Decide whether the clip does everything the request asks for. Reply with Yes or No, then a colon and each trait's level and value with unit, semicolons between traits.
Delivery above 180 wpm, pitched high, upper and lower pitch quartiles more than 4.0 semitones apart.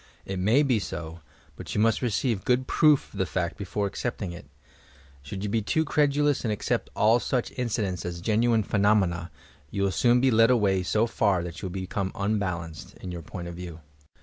No: average, 200 wpm; low, 100 Hz; average, 4.6 semitones